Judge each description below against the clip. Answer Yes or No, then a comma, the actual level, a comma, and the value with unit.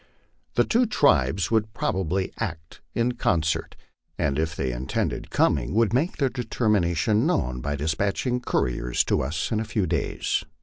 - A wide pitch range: Yes, wide, 7.2 semitones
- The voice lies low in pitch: Yes, very low, 95 Hz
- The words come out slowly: No, average, 150 wpm